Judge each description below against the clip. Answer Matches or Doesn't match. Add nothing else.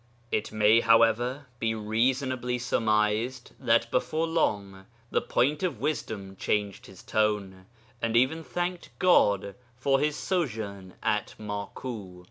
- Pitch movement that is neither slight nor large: Matches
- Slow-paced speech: Matches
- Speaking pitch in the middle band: Doesn't match